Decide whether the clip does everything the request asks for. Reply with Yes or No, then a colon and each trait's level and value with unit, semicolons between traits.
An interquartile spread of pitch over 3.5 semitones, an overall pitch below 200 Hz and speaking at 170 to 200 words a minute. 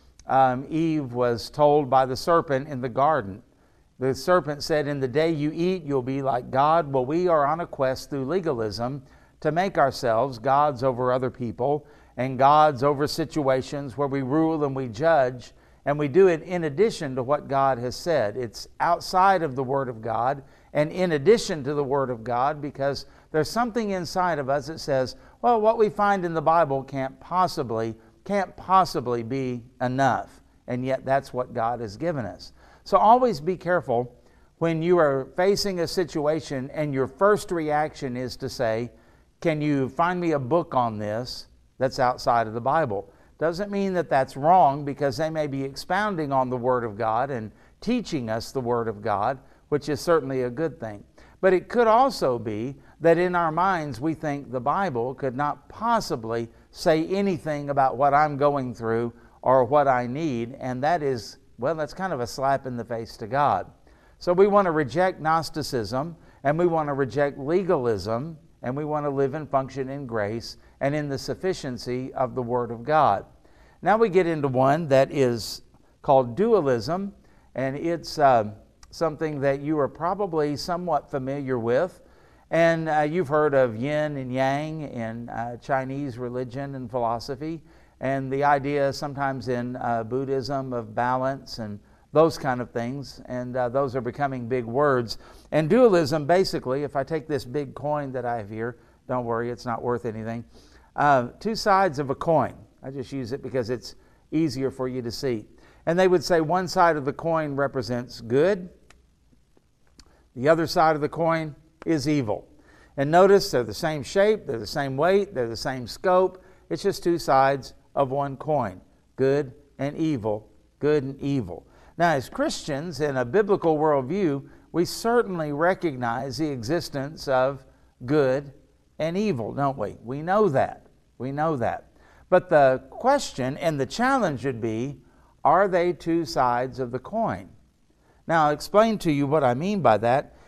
Yes: average, 4.2 semitones; medium, 140 Hz; average, 180 wpm